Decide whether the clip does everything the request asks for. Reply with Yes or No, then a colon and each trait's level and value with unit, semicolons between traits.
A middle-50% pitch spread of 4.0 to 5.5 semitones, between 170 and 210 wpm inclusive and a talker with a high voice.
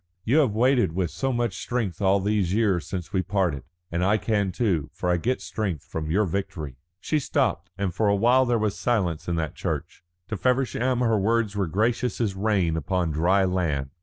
No: average, 4.7 semitones; average, 200 wpm; low, 100 Hz